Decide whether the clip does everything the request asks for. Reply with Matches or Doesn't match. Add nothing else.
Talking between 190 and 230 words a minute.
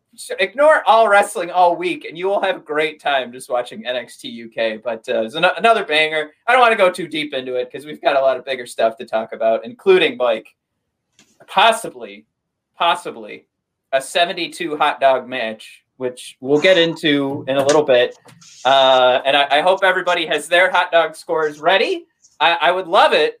Matches